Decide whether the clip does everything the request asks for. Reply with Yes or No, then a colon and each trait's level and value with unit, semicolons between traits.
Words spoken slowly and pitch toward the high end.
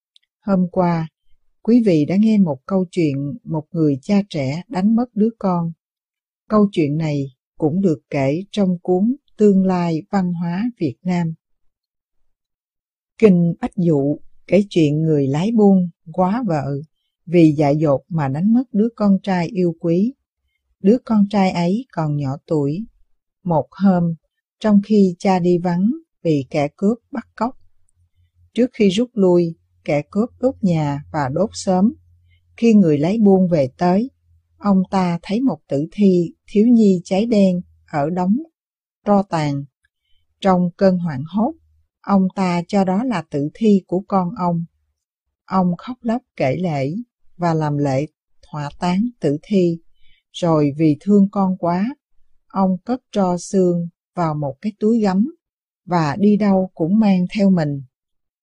No: slow, 155 wpm; medium, 180 Hz